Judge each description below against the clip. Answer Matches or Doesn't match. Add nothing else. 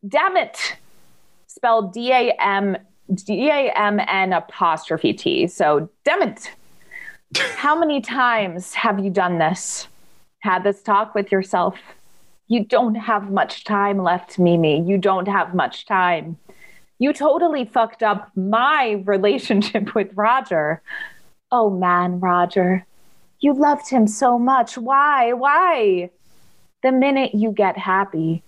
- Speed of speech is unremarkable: Doesn't match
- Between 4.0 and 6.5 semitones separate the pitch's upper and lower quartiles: Matches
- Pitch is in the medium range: Doesn't match